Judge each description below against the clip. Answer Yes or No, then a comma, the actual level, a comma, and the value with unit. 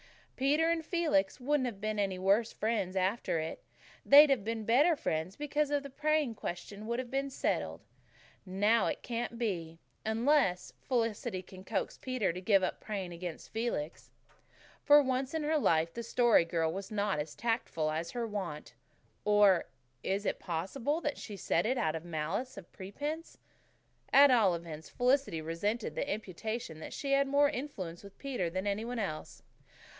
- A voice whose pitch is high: Yes, high, 215 Hz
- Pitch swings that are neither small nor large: No, wide, 6.1 semitones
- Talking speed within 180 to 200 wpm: No, average, 170 wpm